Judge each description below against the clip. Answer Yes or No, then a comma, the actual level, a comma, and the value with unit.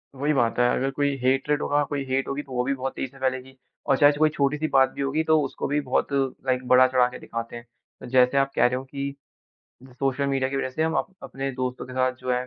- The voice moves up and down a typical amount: No, narrow, 1.6 semitones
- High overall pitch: No, low, 135 Hz